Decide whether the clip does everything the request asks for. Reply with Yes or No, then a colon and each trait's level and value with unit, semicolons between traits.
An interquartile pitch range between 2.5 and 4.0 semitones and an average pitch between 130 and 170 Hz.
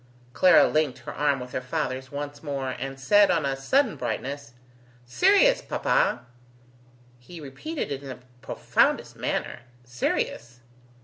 No: average, 4.7 semitones; medium, 140 Hz